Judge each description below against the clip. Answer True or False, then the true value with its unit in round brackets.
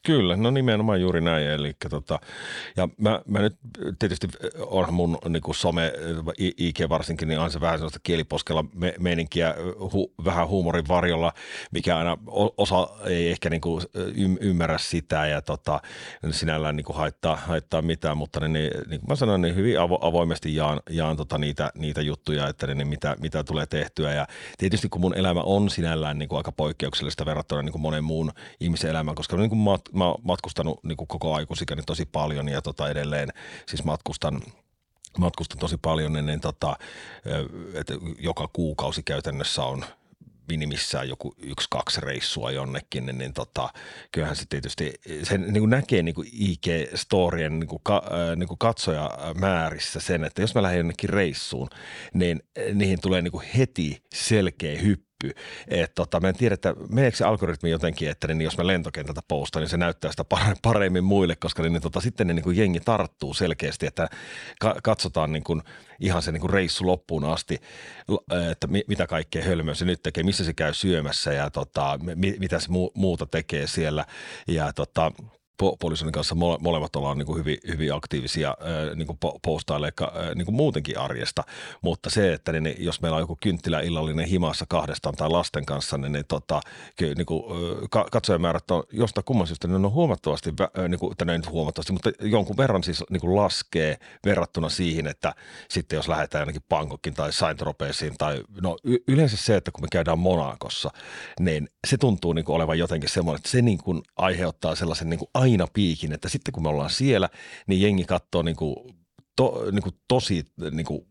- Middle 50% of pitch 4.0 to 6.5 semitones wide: False (3.0 semitones)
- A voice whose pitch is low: True (85 Hz)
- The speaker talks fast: True (170 wpm)